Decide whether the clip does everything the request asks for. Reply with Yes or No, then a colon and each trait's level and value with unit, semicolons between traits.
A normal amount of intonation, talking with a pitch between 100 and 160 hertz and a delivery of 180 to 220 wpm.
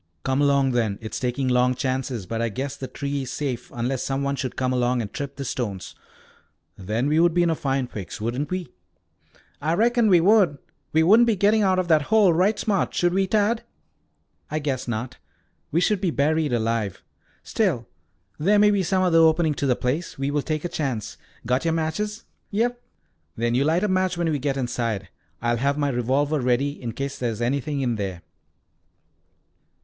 No: wide, 5.8 semitones; medium, 140 Hz; average, 200 wpm